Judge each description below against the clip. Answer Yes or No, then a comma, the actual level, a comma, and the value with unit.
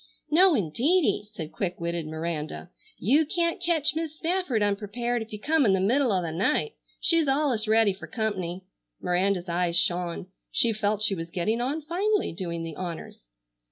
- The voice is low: No, high, 210 Hz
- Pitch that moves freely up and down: Yes, wide, 9.0 semitones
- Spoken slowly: No, average, 170 wpm